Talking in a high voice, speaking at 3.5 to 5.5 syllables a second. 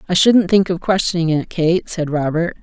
No: medium, 170 Hz; 5.0 syllables/s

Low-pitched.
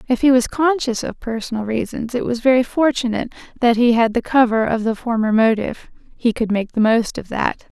No: high, 235 Hz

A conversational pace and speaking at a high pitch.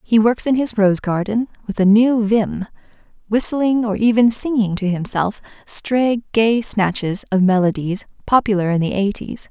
Yes: average, 160 wpm; high, 215 Hz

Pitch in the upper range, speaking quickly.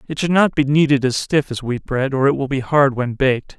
No: low, 135 Hz; fast, 285 wpm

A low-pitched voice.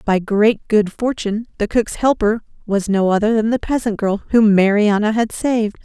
No: high, 215 Hz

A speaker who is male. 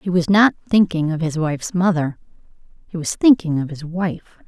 No: female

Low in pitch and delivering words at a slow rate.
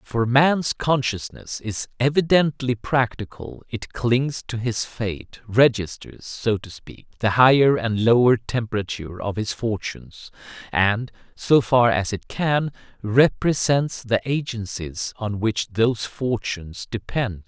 Yes: low, 115 Hz; slow, 125 wpm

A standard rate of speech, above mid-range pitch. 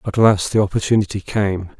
No: average, 165 wpm; low, 100 Hz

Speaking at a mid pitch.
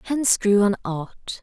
No: high, 210 Hz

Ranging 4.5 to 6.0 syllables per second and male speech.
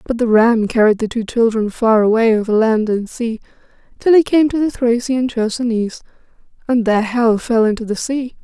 No: 5.4 syllables/s; female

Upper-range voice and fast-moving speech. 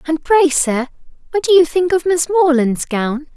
No: very high, 315 Hz; average, 195 wpm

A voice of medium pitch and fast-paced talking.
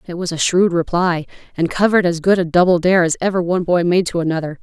Yes: medium, 175 Hz; fast, 245 wpm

